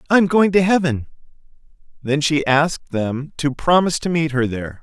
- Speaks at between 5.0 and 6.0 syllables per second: Yes, 5.2 syllables/s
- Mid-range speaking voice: Yes, medium, 150 Hz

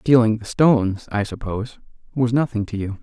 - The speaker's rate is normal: Yes, average, 180 wpm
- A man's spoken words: Yes, male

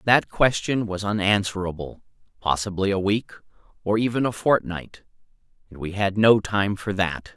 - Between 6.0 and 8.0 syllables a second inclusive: No, 4.8 syllables/s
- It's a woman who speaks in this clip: No, male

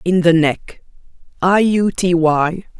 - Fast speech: No, slow, 105 wpm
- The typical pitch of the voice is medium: Yes, medium, 175 Hz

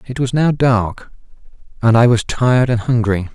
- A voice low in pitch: Yes, low, 120 Hz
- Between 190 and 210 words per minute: No, average, 180 wpm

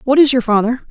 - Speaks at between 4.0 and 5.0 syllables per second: No, 6.6 syllables/s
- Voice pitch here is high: Yes, very high, 250 Hz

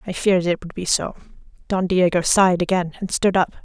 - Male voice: No, female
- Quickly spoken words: Yes, fast, 215 wpm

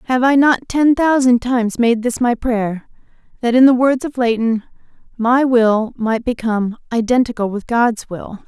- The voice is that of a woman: Yes, female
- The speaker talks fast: No, average, 170 wpm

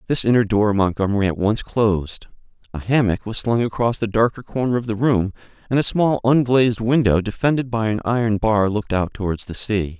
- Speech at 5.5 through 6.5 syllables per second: Yes, 5.6 syllables/s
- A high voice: No, low, 110 Hz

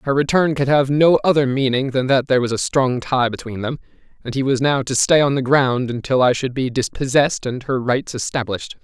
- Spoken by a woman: No, male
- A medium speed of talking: No, fast, 230 wpm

